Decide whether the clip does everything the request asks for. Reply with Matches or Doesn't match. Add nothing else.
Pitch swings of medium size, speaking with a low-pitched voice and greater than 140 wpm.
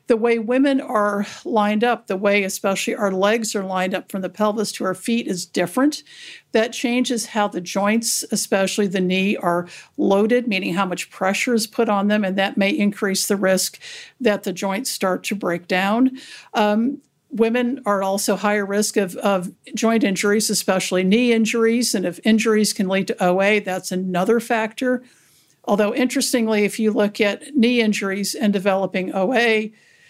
Doesn't match